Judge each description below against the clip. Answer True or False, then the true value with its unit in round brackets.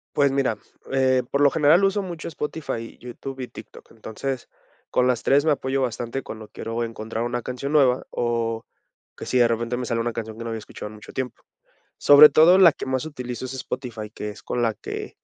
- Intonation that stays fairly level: False (3.2 semitones)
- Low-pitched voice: True (125 Hz)